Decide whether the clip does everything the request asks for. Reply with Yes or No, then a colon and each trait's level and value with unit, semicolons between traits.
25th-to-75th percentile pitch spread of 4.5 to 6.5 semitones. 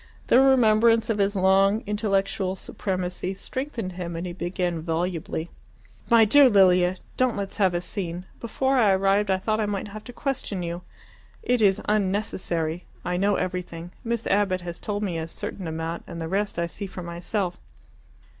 No: average, 3.2 semitones